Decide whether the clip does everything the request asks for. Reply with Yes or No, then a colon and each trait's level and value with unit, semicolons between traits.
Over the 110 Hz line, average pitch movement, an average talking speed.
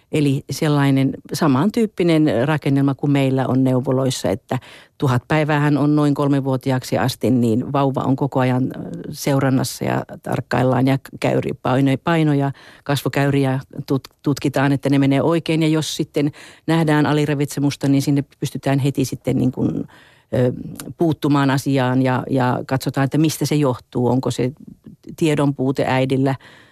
No: medium, 140 Hz; narrow, 2.0 semitones; average, 130 wpm